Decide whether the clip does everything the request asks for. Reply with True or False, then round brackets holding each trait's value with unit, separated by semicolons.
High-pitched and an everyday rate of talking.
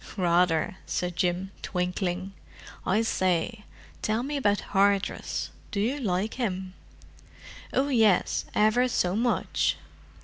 False (195 Hz; 110 wpm)